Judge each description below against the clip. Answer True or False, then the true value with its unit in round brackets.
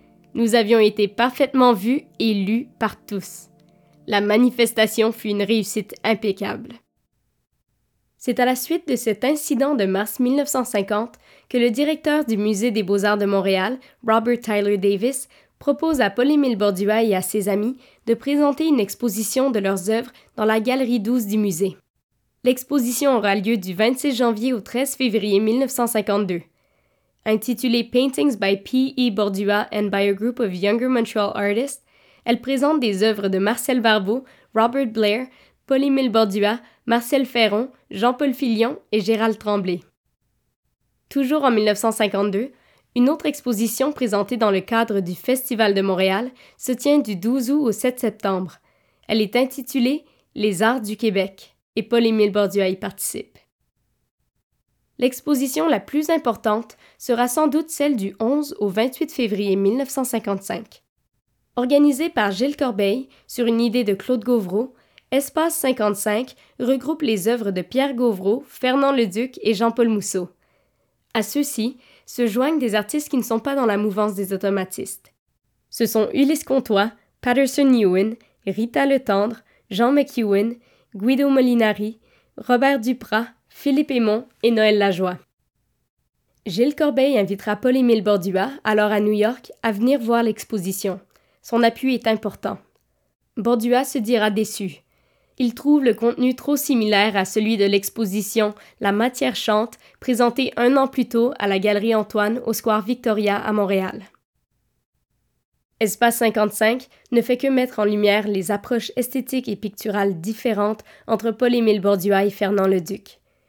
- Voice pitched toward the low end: False (230 Hz)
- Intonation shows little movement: False (3.6 semitones)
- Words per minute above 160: False (145 wpm)